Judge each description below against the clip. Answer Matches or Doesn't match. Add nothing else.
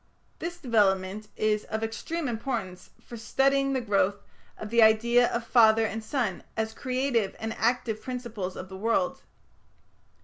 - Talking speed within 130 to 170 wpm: Matches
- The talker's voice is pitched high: Matches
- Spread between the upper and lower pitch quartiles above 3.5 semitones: Doesn't match